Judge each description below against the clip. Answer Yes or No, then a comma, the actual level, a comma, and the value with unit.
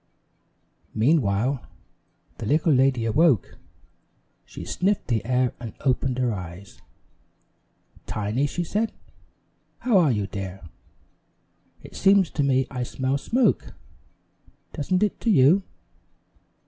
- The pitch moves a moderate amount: No, wide, 6.6 semitones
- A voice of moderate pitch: No, low, 130 Hz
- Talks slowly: Yes, slow, 110 wpm